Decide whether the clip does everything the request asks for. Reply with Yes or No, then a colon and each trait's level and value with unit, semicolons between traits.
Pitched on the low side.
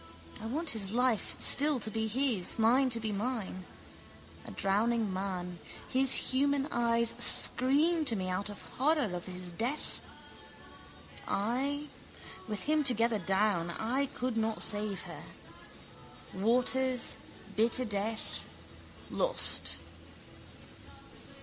No: high, 230 Hz